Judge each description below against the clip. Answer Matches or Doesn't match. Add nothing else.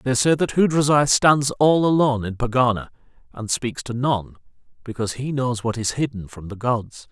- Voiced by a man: Matches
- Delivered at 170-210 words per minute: Matches